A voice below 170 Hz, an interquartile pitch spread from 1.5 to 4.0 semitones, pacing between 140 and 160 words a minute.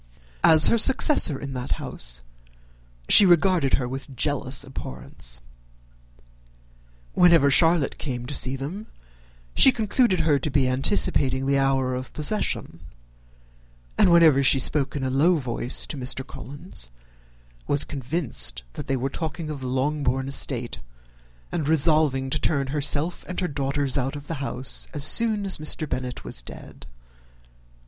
Yes: medium, 140 Hz; average, 3.4 semitones; average, 145 wpm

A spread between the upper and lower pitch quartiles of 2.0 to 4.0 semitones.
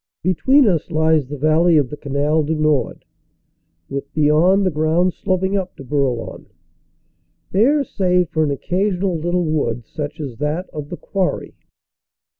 Yes: average, 3.6 semitones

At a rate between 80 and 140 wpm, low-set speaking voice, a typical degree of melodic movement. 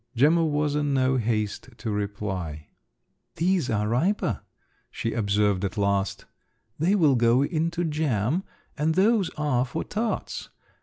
No: slow, 135 wpm; low, 130 Hz; wide, 7.3 semitones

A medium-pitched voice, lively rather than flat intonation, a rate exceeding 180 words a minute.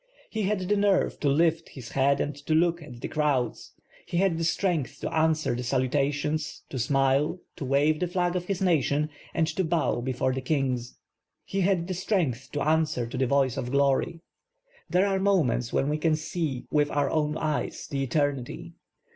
No: medium, 150 Hz; average, 4.0 semitones; average, 190 wpm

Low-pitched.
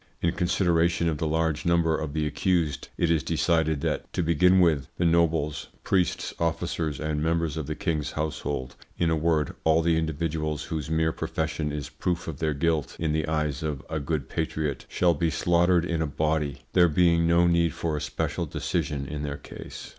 Yes: very low, 80 Hz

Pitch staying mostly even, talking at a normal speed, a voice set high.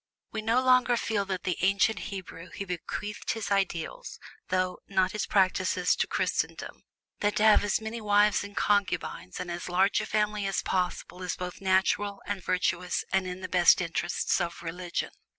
Yes: narrow, 2.3 semitones; average, 175 wpm; high, 195 Hz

